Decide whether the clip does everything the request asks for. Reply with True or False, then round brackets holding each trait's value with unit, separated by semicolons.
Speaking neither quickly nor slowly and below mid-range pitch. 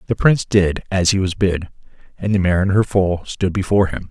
False (235 wpm; 95 Hz)